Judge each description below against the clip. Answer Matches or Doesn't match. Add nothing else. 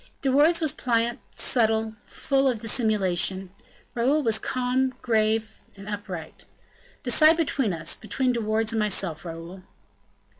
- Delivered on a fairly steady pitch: Doesn't match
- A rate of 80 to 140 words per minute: Matches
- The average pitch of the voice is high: Matches